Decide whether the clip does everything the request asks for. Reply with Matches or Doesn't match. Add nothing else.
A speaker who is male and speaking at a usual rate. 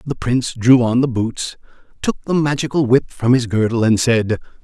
Matches